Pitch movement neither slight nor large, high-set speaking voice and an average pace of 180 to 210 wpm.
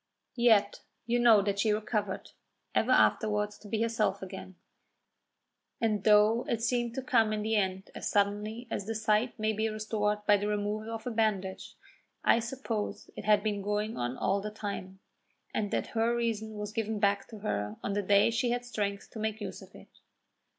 No: narrow, 1.7 semitones; high, 215 Hz; average, 190 wpm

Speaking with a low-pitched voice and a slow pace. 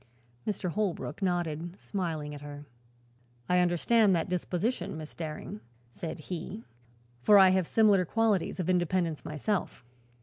No: medium, 180 Hz; slow, 130 wpm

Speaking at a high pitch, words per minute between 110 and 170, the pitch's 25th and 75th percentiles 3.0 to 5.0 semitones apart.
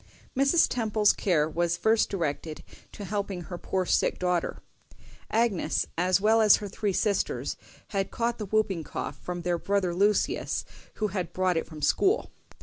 Yes: high, 195 Hz; average, 160 wpm; average, 3.5 semitones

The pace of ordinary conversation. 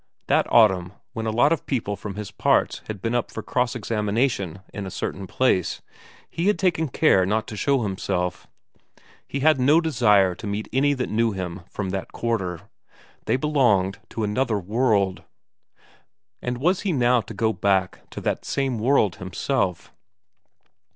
Yes: average, 165 wpm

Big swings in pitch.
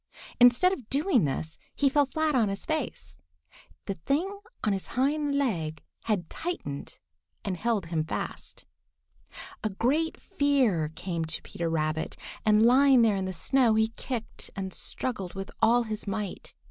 Yes: wide, 7.2 semitones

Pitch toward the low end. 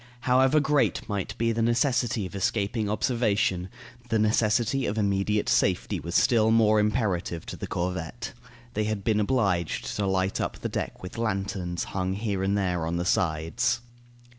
Yes: low, 105 Hz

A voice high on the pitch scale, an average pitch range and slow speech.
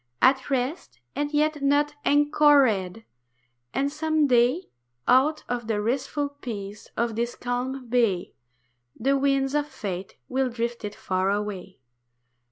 Yes: very high, 255 Hz; average, 4.3 semitones; slow, 130 wpm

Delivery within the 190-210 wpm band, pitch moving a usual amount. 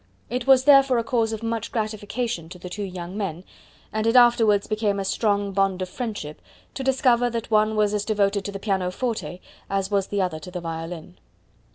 Yes: average, 200 wpm; average, 3.4 semitones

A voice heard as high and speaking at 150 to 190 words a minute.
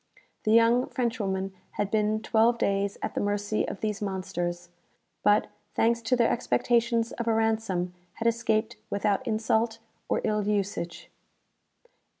No: high, 215 Hz; average, 140 wpm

